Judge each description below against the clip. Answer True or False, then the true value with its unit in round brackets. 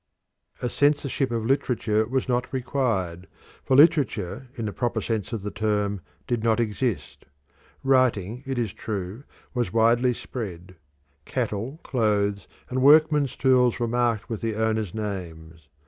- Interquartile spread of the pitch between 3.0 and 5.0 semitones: True (3.8 semitones)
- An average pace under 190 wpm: True (140 wpm)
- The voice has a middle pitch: False (115 Hz)